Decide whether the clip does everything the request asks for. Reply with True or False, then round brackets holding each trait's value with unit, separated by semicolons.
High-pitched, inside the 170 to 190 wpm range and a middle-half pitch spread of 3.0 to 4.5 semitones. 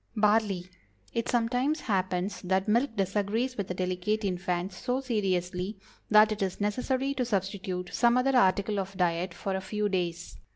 False (200 Hz; 160 wpm; 3.7 semitones)